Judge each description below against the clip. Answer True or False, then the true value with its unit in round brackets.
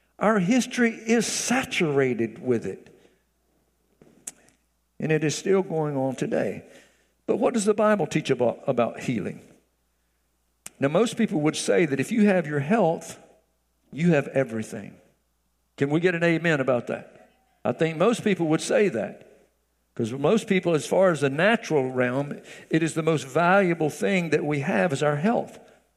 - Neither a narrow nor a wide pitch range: False (6.7 semitones)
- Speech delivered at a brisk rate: False (165 wpm)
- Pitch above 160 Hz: False (155 Hz)